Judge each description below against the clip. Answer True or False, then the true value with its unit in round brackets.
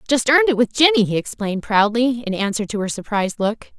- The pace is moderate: False (220 wpm)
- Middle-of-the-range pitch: False (230 Hz)